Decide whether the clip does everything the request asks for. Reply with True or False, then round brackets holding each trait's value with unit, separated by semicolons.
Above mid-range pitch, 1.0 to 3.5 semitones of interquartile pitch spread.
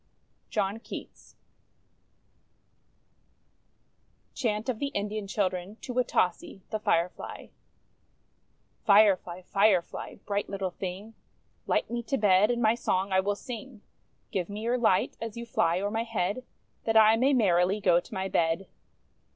True (205 Hz; 3.2 semitones)